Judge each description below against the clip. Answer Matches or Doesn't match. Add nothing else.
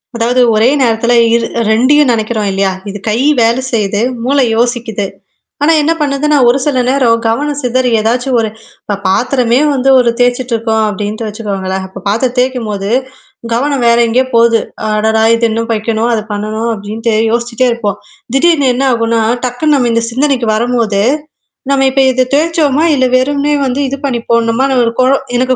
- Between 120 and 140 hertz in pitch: Doesn't match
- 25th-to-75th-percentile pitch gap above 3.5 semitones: Doesn't match